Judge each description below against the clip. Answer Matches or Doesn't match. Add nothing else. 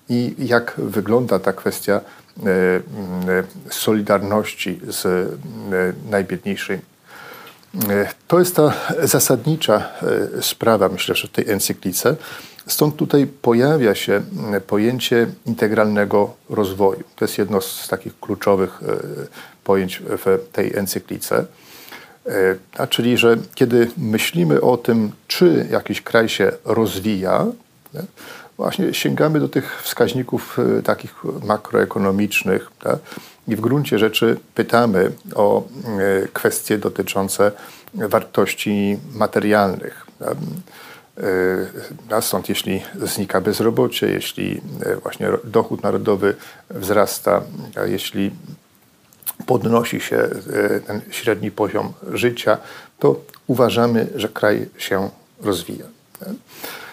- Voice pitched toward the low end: Matches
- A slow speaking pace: Matches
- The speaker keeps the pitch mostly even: Doesn't match